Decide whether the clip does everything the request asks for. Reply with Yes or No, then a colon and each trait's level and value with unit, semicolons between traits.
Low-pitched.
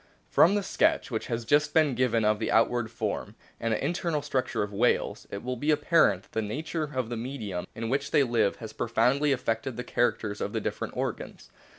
Yes: low, 125 Hz